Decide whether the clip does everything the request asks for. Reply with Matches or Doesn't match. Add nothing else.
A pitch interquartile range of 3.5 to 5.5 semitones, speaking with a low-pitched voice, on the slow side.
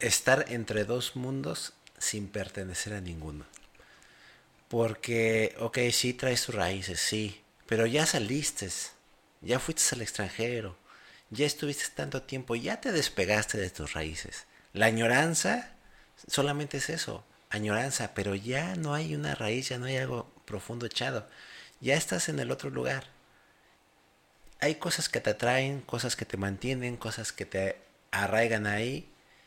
Doesn't match